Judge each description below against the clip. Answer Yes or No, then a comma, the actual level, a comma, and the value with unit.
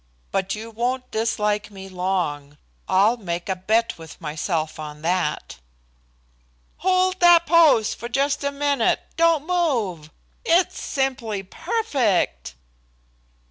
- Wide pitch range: Yes, wide, 7.8 semitones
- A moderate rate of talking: No, slow, 110 wpm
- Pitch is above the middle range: Yes, high, 220 Hz